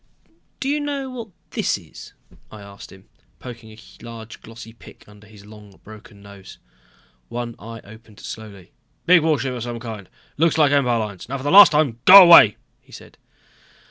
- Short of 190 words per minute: Yes, average, 175 wpm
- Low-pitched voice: Yes, low, 115 Hz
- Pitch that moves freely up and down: Yes, wide, 5.8 semitones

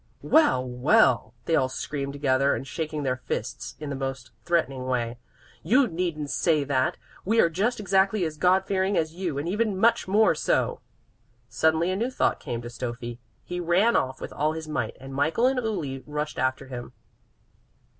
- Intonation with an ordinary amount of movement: No, wide, 6.2 semitones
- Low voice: No, medium, 155 Hz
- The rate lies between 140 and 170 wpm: No, average, 180 wpm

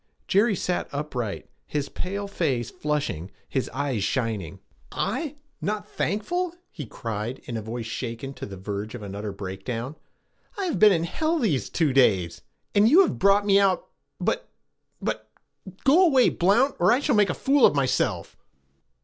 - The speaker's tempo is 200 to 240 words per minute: No, average, 165 wpm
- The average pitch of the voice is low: No, medium, 150 Hz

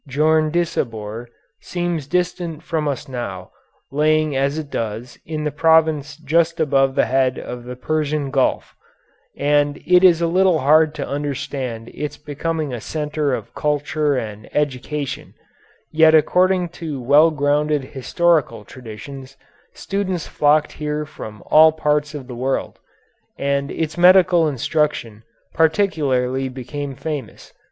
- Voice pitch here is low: No, medium, 150 Hz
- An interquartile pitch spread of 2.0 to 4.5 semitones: Yes, average, 3.1 semitones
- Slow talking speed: Yes, slow, 130 wpm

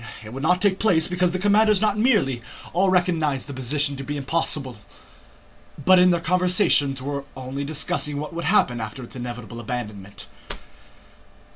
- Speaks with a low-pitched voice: No, medium, 150 Hz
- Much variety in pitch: Yes, wide, 5.8 semitones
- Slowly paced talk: No, average, 160 wpm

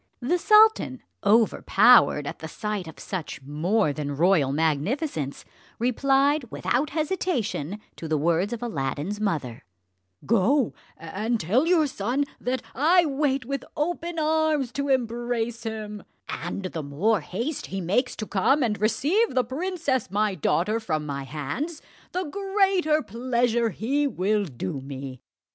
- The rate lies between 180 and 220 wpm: No, average, 140 wpm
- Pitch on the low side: No, high, 225 Hz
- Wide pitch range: Yes, wide, 8.4 semitones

